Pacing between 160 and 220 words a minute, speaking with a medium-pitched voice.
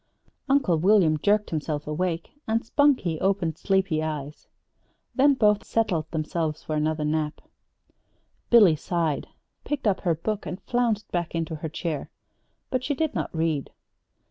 No: average, 145 wpm; medium, 170 Hz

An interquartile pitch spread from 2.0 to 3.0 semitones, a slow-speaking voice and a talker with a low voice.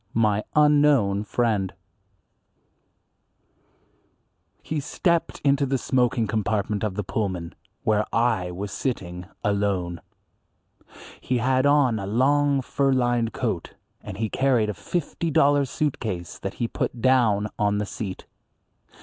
No: average, 5.0 semitones; slow, 130 wpm; low, 115 Hz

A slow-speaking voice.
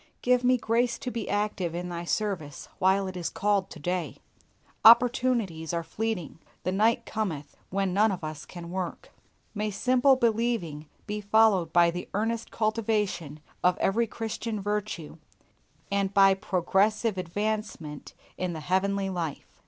No: average, 145 wpm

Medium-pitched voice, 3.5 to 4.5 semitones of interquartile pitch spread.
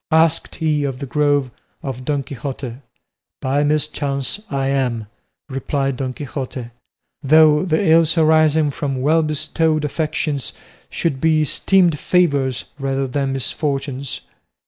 No: medium, 145 Hz; narrow, 2.6 semitones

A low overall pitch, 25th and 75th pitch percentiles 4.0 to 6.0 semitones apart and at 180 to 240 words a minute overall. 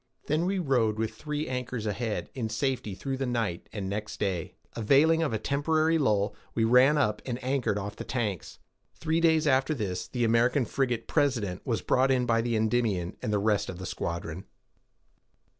Yes: low, 120 Hz; average, 4.5 semitones; average, 185 wpm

